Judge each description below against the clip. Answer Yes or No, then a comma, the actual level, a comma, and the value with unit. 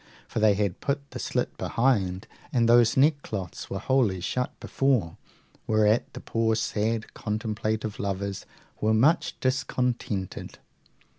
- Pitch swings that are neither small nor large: Yes, average, 3.7 semitones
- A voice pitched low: Yes, low, 110 Hz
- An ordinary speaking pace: No, slow, 125 wpm